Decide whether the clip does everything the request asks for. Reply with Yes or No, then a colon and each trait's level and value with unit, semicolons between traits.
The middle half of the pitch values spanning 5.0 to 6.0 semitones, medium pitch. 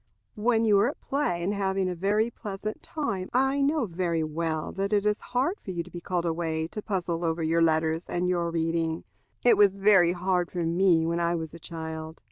No: average, 3.8 semitones; medium, 180 Hz